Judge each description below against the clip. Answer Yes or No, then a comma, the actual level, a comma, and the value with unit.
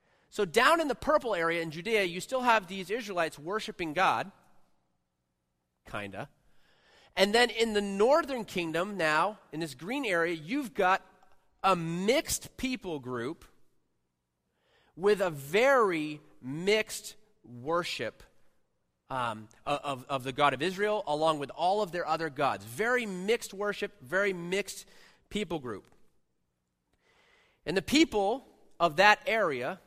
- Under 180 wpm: Yes, slow, 135 wpm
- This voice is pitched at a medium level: Yes, medium, 180 Hz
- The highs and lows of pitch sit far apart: Yes, wide, 6.8 semitones